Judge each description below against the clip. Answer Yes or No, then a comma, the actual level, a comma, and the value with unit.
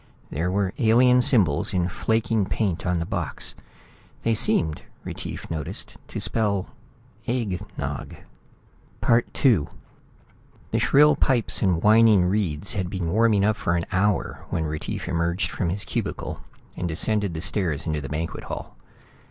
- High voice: No, very low, 95 Hz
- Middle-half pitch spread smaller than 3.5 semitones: No, average, 4.7 semitones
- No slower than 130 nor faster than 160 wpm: Yes, average, 145 wpm